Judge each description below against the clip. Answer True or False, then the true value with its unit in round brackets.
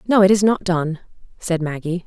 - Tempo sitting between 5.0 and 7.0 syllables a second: True (5.2 syllables/s)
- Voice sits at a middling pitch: True (180 Hz)